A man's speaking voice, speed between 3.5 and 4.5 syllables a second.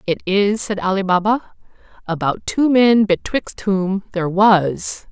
No: female; 4.1 syllables/s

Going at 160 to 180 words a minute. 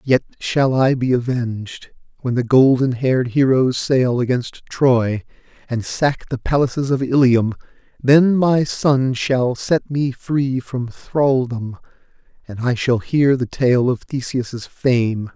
No: average, 145 wpm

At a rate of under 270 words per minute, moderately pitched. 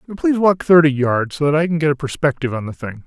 No: fast, 275 wpm; medium, 150 Hz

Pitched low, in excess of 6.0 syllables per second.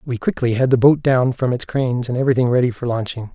Yes: low, 125 Hz; 6.5 syllables/s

